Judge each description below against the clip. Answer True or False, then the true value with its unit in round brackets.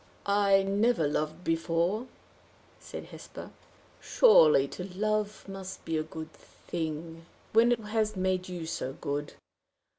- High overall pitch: False (180 Hz)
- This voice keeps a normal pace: False (125 wpm)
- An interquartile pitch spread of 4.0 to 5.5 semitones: True (4.5 semitones)